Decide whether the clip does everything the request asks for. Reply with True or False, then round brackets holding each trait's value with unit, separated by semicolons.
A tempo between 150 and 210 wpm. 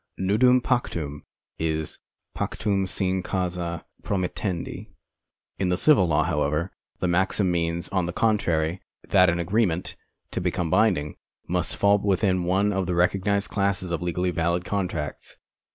False (140 wpm)